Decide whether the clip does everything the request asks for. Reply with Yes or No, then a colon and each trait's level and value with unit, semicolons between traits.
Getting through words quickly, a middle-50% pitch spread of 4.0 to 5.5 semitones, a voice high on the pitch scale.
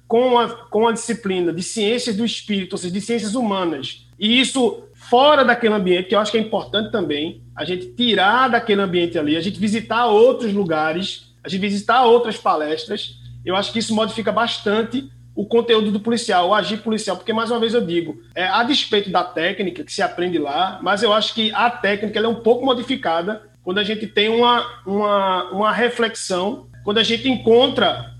Yes: fast, 200 wpm; average, 4.3 semitones; high, 215 Hz